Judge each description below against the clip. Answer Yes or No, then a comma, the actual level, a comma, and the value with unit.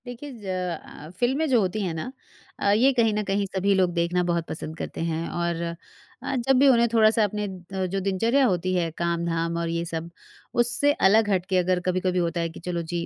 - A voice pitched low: No, medium, 185 Hz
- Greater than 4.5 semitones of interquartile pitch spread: No, average, 4.2 semitones